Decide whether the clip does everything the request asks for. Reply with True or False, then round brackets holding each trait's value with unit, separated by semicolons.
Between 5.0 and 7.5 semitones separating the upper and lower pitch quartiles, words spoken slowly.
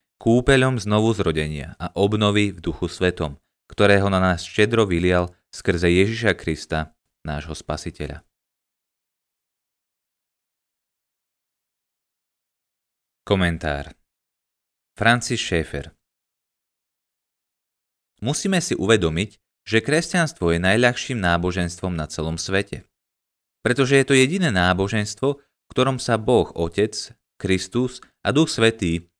True (5.4 semitones; 95 wpm)